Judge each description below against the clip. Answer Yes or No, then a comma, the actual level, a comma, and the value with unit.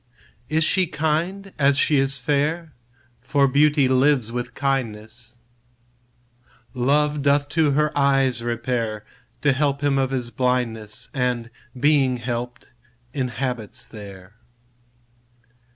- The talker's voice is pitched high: No, low, 135 Hz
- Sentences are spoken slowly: Yes, slow, 110 wpm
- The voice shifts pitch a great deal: No, average, 3.2 semitones